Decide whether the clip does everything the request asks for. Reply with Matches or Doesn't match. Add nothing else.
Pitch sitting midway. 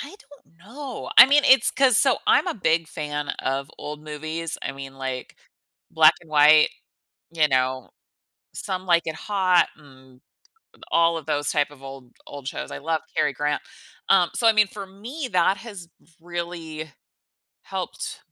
Matches